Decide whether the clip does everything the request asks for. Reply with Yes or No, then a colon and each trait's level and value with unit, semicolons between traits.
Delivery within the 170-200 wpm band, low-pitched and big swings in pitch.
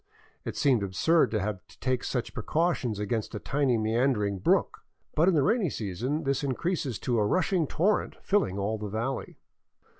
Yes: average, 180 wpm; low, 125 Hz; wide, 6.3 semitones